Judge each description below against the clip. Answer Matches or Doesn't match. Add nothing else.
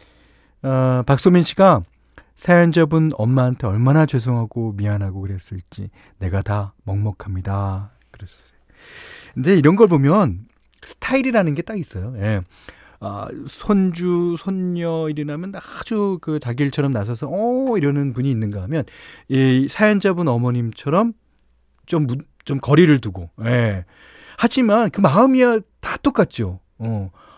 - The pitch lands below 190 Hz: Matches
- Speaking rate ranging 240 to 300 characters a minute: Matches